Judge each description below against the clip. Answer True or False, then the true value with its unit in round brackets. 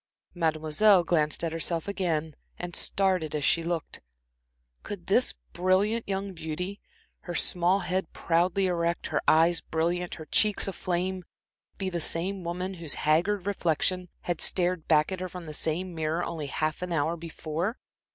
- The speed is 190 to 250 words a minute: False (155 wpm)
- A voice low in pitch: False (175 Hz)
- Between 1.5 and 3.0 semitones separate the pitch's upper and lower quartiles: True (2.5 semitones)